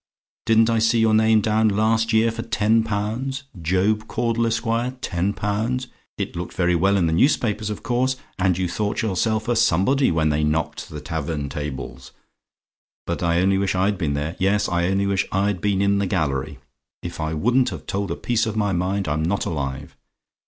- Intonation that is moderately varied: Yes, average, 4.5 semitones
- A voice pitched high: No, low, 100 Hz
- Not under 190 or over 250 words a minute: Yes, average, 195 wpm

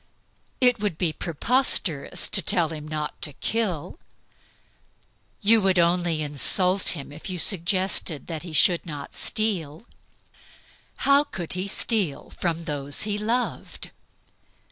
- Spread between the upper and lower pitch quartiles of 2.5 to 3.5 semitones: No, average, 5.0 semitones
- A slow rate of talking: Yes, slow, 125 wpm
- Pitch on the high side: No, medium, 175 Hz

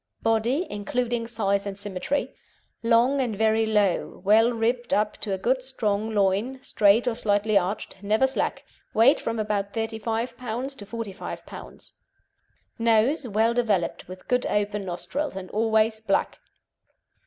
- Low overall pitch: No, high, 220 Hz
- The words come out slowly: No, average, 145 wpm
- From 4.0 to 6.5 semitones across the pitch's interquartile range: No, average, 2.7 semitones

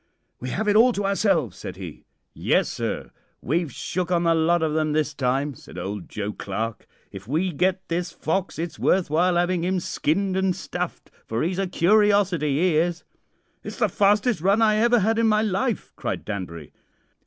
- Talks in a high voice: No, medium, 175 Hz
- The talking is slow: No, average, 190 wpm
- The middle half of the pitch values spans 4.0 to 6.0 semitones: Yes, average, 4.6 semitones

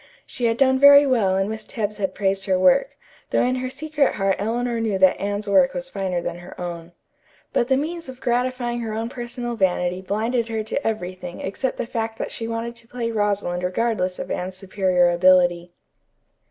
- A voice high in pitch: Yes, high, 220 Hz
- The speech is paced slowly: No, average, 195 wpm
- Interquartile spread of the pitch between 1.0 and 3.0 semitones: No, average, 4.5 semitones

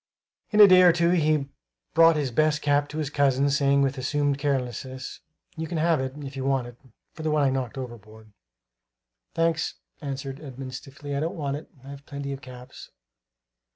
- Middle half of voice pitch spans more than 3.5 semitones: No, narrow, 2.6 semitones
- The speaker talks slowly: No, average, 190 wpm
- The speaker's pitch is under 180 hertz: Yes, medium, 140 Hz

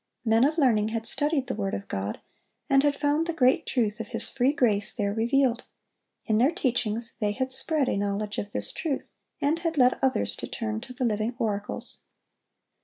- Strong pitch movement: No, average, 4.3 semitones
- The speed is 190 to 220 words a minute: Yes, average, 195 wpm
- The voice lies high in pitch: Yes, high, 240 Hz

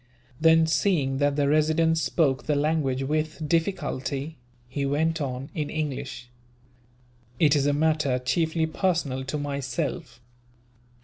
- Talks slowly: Yes, slow, 125 wpm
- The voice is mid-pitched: Yes, medium, 150 Hz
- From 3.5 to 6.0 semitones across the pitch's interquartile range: No, average, 2.7 semitones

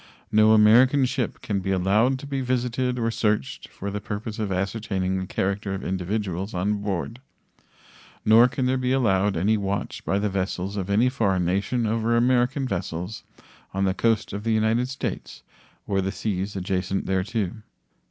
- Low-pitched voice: Yes, low, 105 Hz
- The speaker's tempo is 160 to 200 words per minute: Yes, average, 170 wpm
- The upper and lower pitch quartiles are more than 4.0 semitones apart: No, average, 3.4 semitones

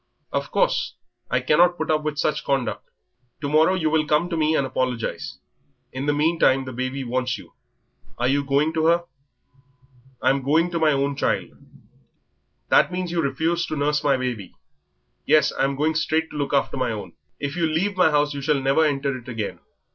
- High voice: No, medium, 145 Hz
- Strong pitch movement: No, average, 2.9 semitones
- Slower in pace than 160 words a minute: No, average, 200 wpm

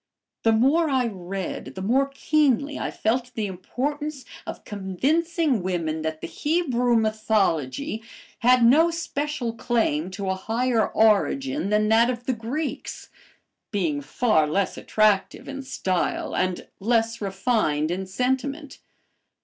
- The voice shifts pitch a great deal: Yes, wide, 6.0 semitones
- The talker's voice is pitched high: Yes, high, 230 Hz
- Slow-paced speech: Yes, slow, 130 wpm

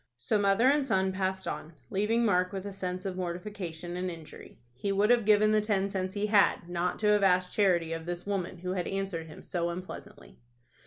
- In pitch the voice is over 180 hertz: Yes, high, 190 Hz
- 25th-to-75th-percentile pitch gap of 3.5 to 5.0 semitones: No, narrow, 2.5 semitones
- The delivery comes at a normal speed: No, fast, 210 wpm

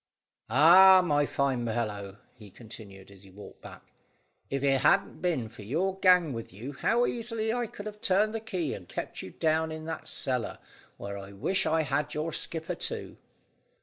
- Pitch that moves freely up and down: Yes, wide, 8.7 semitones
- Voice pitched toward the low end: No, medium, 150 Hz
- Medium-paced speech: Yes, average, 180 wpm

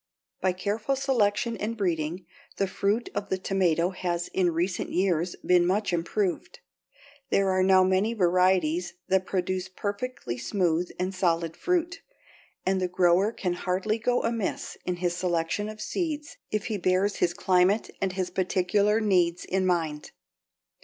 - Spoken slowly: No, average, 150 wpm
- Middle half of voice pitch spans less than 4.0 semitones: Yes, average, 2.7 semitones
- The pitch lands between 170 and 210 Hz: Yes, medium, 185 Hz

